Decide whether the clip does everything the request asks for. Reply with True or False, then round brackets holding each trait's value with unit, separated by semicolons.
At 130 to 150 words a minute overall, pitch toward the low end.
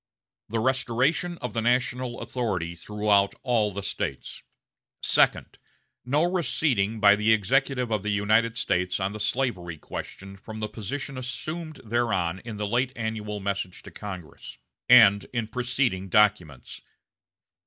True (135 wpm; 110 Hz)